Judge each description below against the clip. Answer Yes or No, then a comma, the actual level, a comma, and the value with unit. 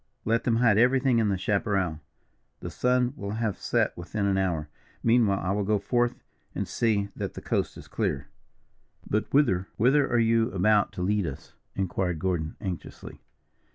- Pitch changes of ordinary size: Yes, average, 3.7 semitones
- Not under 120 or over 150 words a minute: No, average, 170 wpm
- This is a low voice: Yes, low, 105 Hz